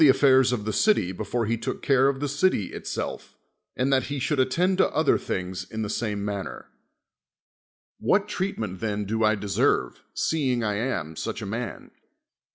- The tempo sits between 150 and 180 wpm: Yes, average, 175 wpm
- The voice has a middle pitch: No, low, 115 Hz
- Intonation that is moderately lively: Yes, average, 4.9 semitones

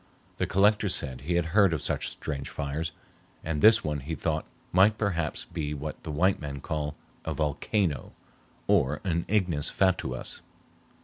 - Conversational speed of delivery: Yes, average, 160 wpm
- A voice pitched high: No, very low, 80 Hz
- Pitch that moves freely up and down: No, average, 4.1 semitones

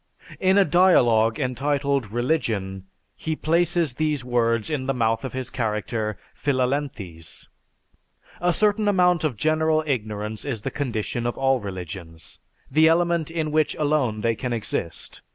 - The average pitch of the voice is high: No, low, 130 Hz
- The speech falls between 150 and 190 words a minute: No, average, 140 wpm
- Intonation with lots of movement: Yes, wide, 5.9 semitones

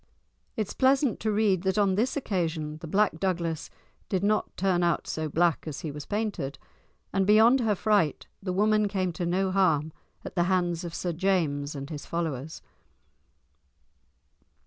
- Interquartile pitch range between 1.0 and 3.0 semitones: No, average, 4.3 semitones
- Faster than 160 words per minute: Yes, average, 170 wpm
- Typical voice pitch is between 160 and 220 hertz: Yes, medium, 185 Hz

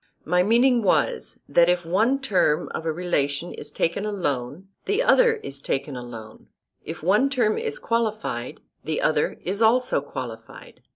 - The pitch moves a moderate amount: No, wide, 8.1 semitones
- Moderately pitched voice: Yes, medium, 180 Hz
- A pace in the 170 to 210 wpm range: No, average, 155 wpm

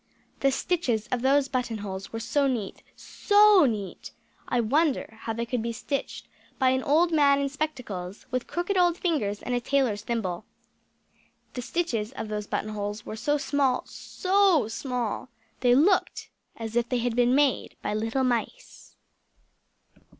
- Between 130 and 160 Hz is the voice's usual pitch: No, very high, 250 Hz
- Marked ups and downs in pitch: No, average, 4.6 semitones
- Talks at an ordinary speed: Yes, average, 160 wpm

